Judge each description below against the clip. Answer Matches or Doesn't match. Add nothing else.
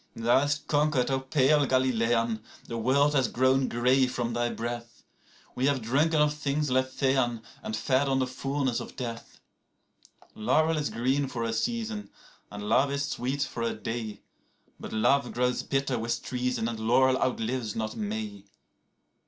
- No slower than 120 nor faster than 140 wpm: Doesn't match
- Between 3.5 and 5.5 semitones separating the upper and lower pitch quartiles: Doesn't match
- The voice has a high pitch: Doesn't match